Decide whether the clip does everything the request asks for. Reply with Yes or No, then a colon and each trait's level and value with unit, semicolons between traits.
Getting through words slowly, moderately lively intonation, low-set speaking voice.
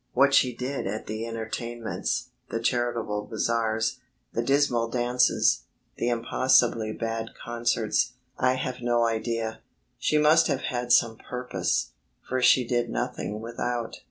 No: slow, 130 wpm; narrow, 1.7 semitones; low, 120 Hz